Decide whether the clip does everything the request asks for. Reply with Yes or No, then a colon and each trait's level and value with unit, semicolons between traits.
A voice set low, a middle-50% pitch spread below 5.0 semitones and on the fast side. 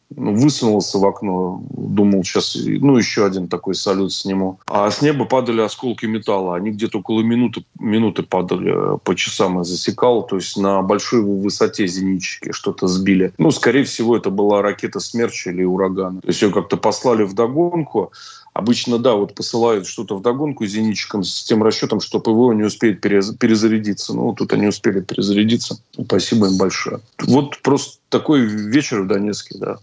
Yes: low, 105 Hz; average, 3.2 semitones; fast, 165 wpm